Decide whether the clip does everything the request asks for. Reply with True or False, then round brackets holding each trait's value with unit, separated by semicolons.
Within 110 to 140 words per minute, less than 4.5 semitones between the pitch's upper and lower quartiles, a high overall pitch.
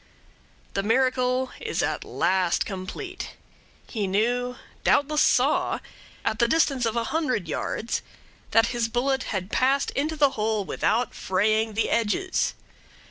True (135 wpm; 3.8 semitones; 235 Hz)